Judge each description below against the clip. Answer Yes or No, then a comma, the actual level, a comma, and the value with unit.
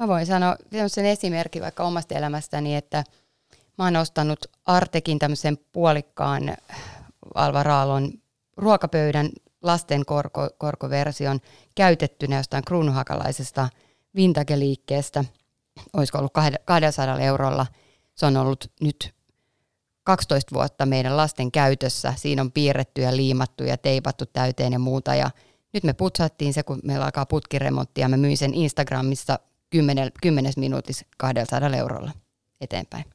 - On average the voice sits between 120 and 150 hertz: Yes, medium, 140 Hz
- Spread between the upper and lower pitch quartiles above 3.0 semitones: No, narrow, 2.6 semitones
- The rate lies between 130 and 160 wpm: No, average, 120 wpm